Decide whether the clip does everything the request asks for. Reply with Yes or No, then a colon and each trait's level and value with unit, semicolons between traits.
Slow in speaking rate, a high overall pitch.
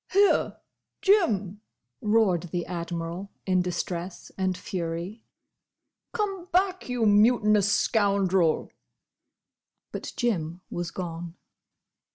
Yes: slow, 90 wpm; high, 195 Hz